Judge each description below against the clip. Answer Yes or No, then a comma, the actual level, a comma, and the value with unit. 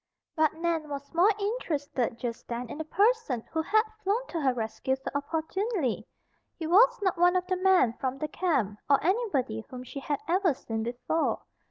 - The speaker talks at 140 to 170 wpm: No, average, 185 wpm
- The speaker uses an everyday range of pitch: No, wide, 6.3 semitones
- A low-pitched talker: No, very high, 315 Hz